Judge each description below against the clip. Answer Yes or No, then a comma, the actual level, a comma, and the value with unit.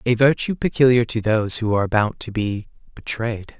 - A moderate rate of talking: Yes, average, 185 wpm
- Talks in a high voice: No, low, 115 Hz